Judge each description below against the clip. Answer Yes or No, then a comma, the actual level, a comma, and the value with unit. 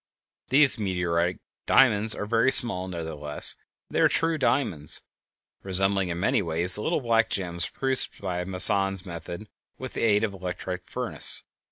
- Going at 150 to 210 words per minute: Yes, average, 160 wpm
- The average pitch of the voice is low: Yes, very low, 95 Hz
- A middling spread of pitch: Yes, average, 4.3 semitones